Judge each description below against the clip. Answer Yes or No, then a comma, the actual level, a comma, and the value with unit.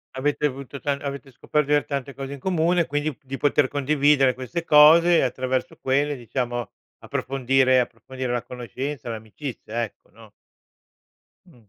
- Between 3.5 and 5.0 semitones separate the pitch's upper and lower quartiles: No, average, 2.7 semitones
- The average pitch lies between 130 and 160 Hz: Yes, low, 135 Hz